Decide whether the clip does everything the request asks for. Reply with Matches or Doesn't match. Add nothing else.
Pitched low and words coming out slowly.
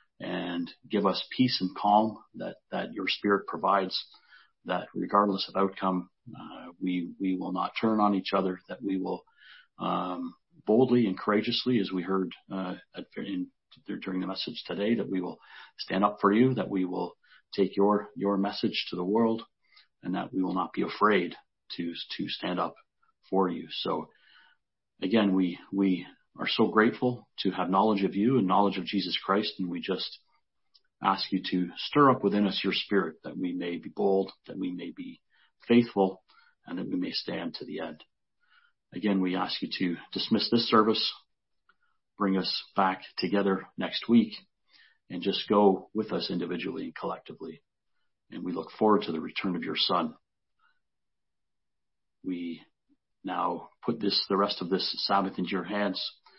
Doesn't match